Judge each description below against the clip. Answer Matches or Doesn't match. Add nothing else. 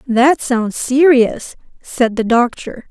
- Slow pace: Matches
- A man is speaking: Doesn't match